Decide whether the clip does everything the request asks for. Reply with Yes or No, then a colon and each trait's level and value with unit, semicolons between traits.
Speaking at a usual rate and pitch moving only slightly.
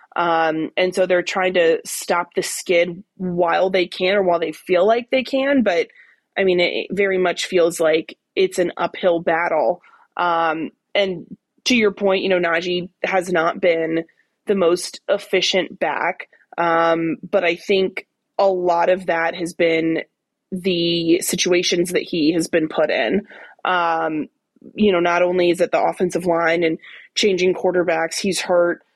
Yes: average, 165 wpm; narrow, 2.2 semitones